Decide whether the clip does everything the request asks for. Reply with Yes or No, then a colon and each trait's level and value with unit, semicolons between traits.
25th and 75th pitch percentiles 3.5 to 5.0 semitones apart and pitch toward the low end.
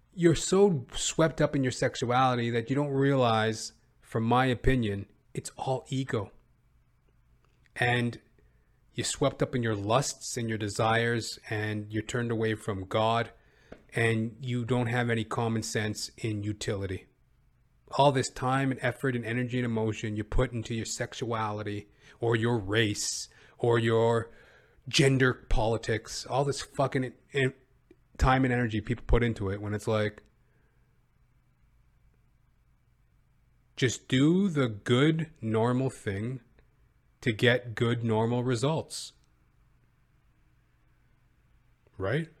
No: average, 2.8 semitones; low, 120 Hz